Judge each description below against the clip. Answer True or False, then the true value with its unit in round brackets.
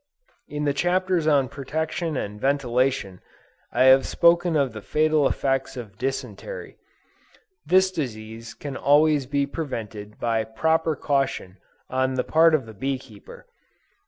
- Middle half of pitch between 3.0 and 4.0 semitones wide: False (4.7 semitones)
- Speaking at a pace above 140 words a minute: False (135 wpm)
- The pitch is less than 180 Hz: True (135 Hz)